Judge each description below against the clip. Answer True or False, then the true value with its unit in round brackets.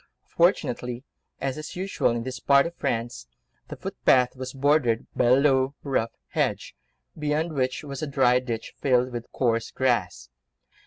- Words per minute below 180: True (145 wpm)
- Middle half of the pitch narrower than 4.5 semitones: True (2.9 semitones)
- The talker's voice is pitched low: True (130 Hz)